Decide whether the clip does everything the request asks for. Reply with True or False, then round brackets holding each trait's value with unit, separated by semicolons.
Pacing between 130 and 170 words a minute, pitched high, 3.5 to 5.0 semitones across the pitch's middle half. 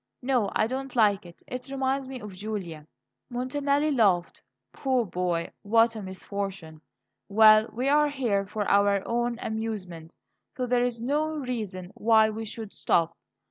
True (150 wpm; 220 Hz; 4.3 semitones)